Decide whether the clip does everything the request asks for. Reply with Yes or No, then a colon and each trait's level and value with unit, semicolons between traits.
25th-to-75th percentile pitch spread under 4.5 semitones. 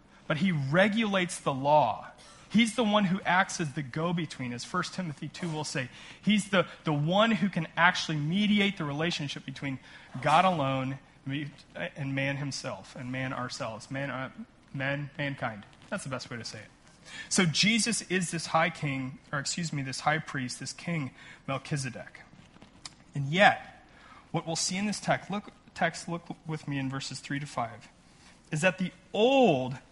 No: average, 5.3 semitones